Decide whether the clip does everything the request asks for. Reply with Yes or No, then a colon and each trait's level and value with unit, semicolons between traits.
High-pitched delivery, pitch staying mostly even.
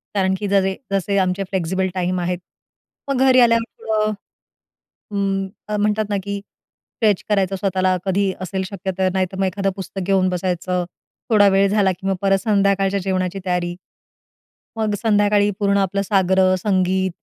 Yes: high, 195 Hz; narrow, 1.5 semitones